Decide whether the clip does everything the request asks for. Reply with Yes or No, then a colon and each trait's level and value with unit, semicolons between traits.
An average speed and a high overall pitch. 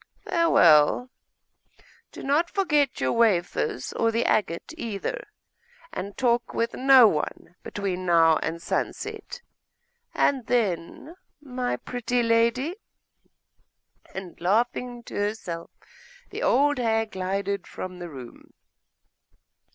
No: slow, 105 wpm; high, 230 Hz